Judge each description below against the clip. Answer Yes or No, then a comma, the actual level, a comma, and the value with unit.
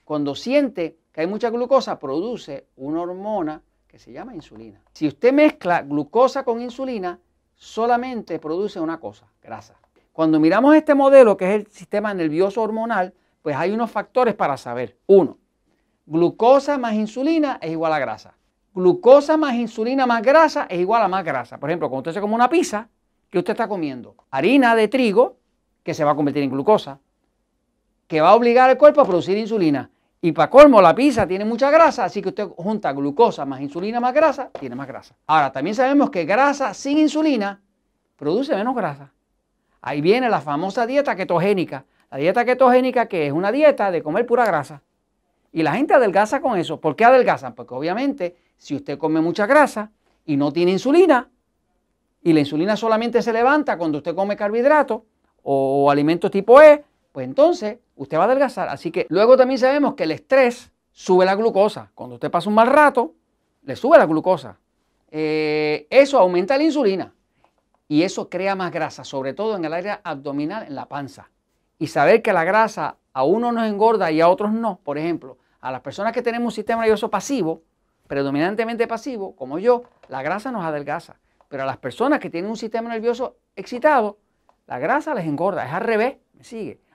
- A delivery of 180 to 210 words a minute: Yes, average, 185 wpm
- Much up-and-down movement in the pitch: Yes, wide, 7.6 semitones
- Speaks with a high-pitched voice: Yes, high, 205 Hz